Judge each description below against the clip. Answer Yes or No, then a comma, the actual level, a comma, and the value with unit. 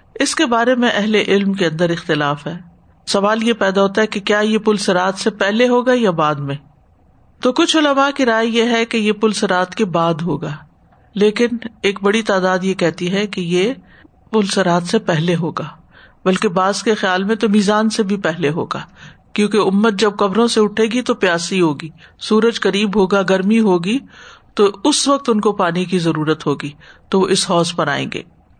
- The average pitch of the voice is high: Yes, high, 200 Hz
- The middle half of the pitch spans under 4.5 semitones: Yes, average, 4.1 semitones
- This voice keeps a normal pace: No, fast, 200 wpm